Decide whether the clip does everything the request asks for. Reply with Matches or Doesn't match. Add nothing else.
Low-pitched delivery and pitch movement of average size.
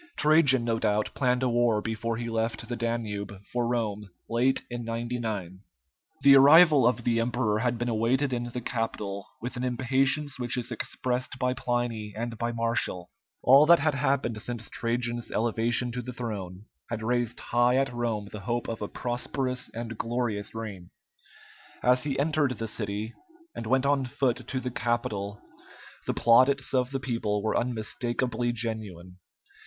Doesn't match